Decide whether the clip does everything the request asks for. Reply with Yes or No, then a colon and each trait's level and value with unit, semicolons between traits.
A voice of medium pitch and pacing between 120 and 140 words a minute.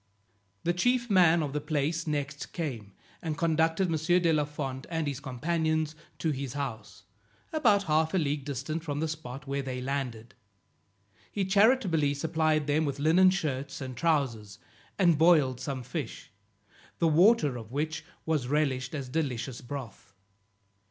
No: medium, 150 Hz; average, 155 wpm